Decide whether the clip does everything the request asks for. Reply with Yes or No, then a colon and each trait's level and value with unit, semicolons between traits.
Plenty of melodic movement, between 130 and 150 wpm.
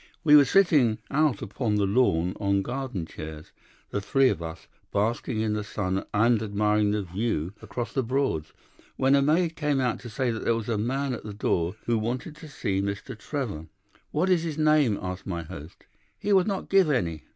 No: wide, 5.9 semitones; average, 200 wpm